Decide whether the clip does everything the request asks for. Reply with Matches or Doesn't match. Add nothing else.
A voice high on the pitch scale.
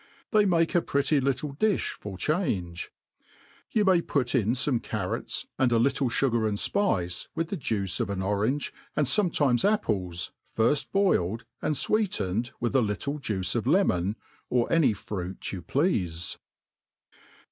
Doesn't match